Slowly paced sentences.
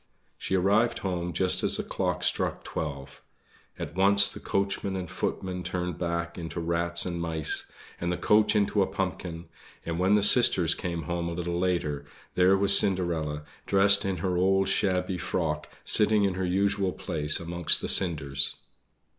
No: average, 165 wpm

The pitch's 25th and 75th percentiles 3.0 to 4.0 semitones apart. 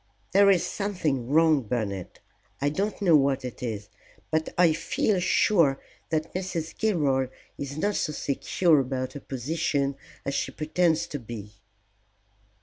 No: average, 4.4 semitones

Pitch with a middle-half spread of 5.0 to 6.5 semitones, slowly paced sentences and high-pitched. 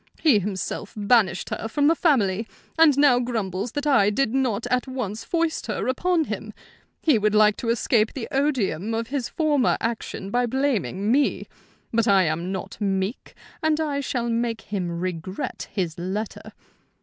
No: wide, 5.5 semitones; average, 165 wpm; high, 230 Hz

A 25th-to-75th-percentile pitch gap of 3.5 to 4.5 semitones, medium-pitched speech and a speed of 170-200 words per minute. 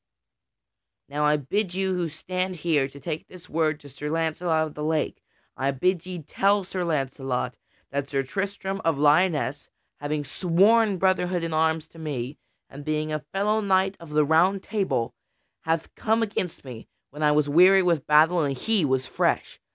Yes: average, 4.1 semitones; medium, 160 Hz; average, 180 wpm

